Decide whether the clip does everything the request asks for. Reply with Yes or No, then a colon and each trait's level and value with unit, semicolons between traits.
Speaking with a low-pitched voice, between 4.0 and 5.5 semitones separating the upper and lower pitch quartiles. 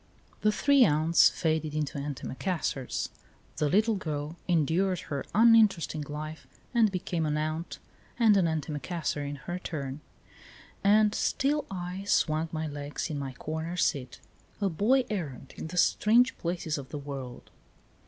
No: medium, 160 Hz; average, 4.8 semitones